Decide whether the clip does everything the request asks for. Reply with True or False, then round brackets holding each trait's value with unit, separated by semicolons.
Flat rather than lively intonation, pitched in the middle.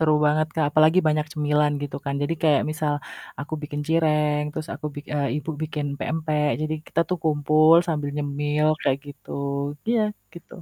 True (1.1 semitones; 150 Hz)